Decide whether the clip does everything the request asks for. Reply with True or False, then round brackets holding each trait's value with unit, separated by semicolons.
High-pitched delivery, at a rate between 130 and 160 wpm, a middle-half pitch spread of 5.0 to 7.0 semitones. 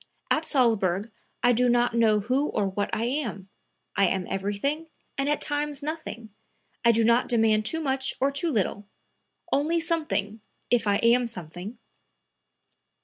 True (235 Hz; 150 wpm; 5.3 semitones)